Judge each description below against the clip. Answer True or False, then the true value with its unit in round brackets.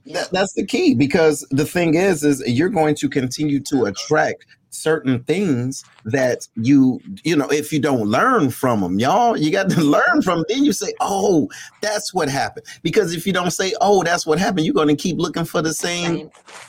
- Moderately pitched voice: True (160 Hz)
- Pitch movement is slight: False (4.4 semitones)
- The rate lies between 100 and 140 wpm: False (205 wpm)